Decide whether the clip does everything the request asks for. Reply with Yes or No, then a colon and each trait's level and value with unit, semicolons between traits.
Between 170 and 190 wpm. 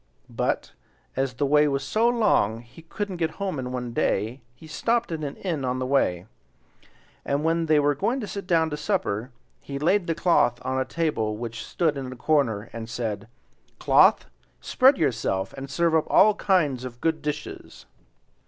Yes: average, 185 wpm